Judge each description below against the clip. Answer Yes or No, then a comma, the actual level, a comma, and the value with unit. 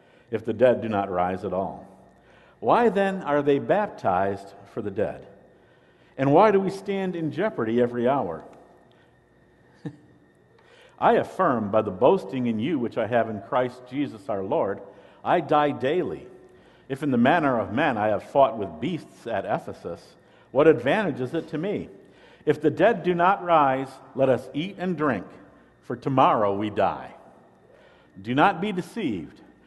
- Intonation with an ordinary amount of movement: No, wide, 7.5 semitones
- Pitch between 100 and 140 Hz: Yes, low, 135 Hz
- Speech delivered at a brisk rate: No, average, 165 wpm